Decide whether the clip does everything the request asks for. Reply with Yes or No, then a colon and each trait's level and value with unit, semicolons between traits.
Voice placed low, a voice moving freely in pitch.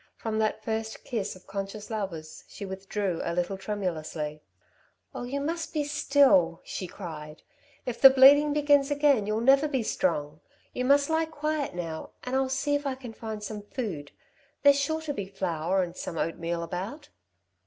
No: high, 220 Hz; wide, 7.7 semitones